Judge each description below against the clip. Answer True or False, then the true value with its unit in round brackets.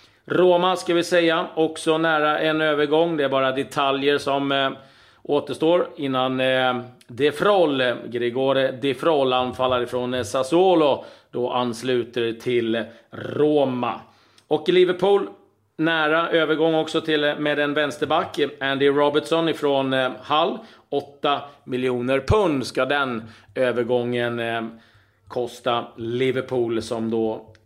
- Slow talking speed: True (120 wpm)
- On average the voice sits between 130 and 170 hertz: True (135 Hz)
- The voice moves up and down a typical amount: True (3.9 semitones)